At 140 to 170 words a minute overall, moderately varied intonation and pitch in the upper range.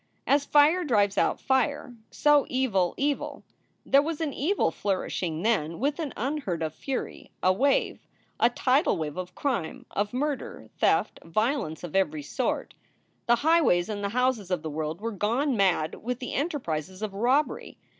No: average, 165 wpm; wide, 7.4 semitones; high, 230 Hz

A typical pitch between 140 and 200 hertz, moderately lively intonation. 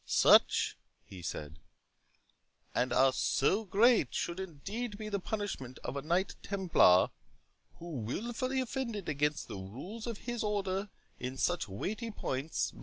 No: high, 190 Hz; wide, 8.3 semitones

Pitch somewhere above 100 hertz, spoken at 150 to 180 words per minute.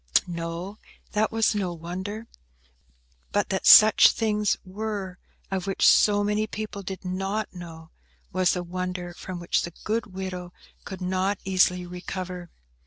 No: medium, 185 Hz; average, 140 wpm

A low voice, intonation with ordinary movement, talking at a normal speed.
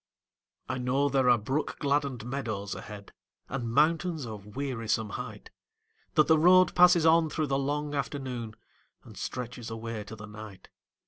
Yes: low, 130 Hz; average, 4.9 semitones; average, 150 wpm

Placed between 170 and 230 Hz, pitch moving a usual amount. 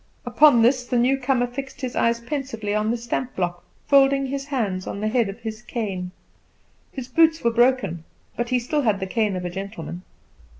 No: high, 240 Hz; average, 4.2 semitones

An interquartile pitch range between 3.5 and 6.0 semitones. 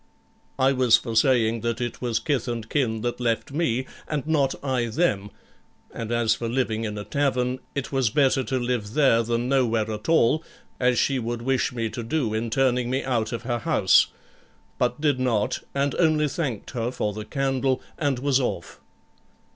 No: average, 2.8 semitones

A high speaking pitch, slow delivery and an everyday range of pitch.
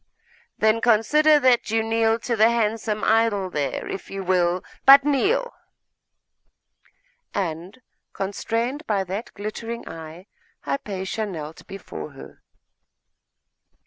Yes: high, 215 Hz; slow, 110 wpm; average, 3.7 semitones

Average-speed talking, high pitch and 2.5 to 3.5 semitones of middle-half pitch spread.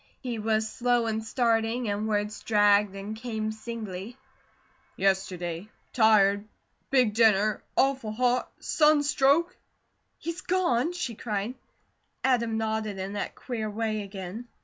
No: slow, 125 wpm; high, 220 Hz; average, 2.9 semitones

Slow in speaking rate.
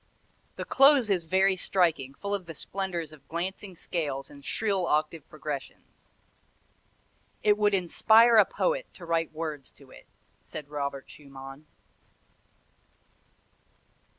Yes: slow, 125 wpm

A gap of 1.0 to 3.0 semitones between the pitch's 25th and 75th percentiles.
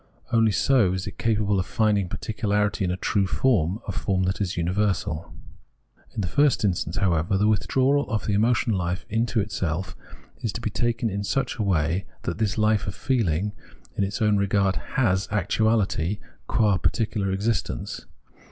Yes: average, 2.7 semitones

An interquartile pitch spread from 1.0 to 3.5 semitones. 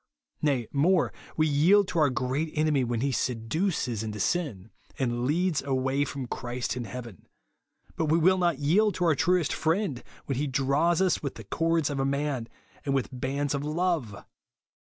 No: average, 4.6 semitones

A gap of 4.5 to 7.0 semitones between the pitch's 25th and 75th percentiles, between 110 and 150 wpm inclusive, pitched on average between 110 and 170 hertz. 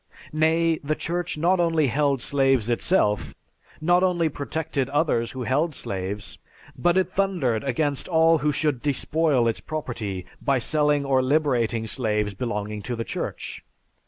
Yes: average, 5.3 semitones; average, 145 wpm; medium, 140 Hz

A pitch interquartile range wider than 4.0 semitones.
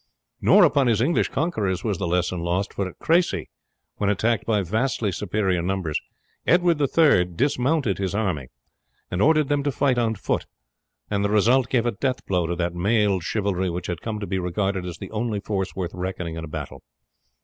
Yes: average, 5.1 semitones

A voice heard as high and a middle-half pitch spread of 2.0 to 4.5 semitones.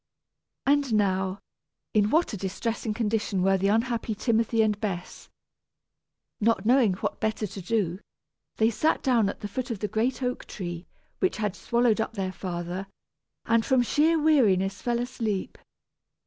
Yes: high, 220 Hz; average, 3.6 semitones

